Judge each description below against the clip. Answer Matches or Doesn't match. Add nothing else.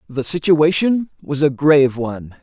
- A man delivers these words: Matches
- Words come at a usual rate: Matches